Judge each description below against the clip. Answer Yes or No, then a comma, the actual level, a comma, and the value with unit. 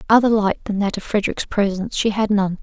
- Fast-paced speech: Yes, fast, 230 wpm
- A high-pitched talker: Yes, high, 205 Hz